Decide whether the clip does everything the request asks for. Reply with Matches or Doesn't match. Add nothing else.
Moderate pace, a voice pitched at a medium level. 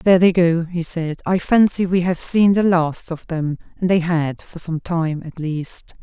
Doesn't match